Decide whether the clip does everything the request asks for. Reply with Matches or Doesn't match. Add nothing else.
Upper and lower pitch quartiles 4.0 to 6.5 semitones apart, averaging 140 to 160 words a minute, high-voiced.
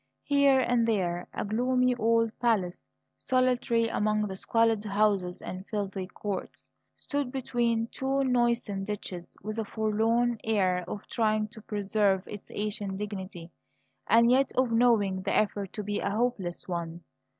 Doesn't match